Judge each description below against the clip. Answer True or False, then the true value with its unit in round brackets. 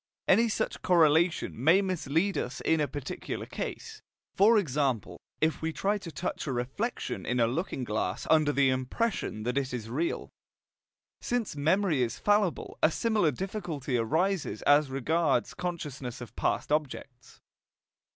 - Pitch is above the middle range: False (150 Hz)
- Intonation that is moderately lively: False (6.0 semitones)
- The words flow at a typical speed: True (145 wpm)